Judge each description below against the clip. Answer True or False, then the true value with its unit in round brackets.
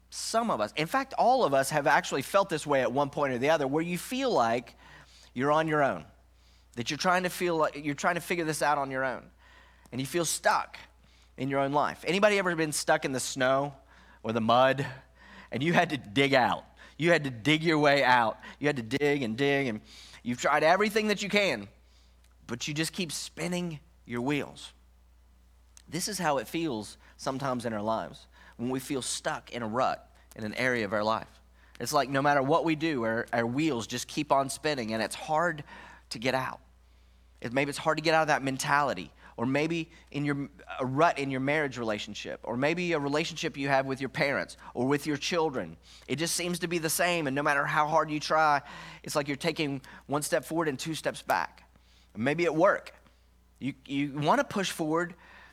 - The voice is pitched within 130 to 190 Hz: True (140 Hz)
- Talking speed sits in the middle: False (220 wpm)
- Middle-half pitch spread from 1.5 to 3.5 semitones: False (5.3 semitones)